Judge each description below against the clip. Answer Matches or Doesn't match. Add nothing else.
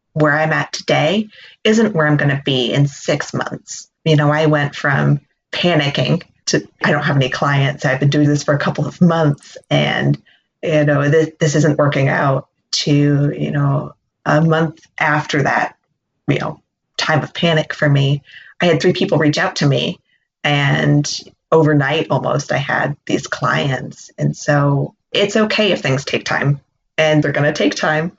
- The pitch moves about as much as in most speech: Doesn't match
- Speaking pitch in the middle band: Matches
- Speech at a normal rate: Matches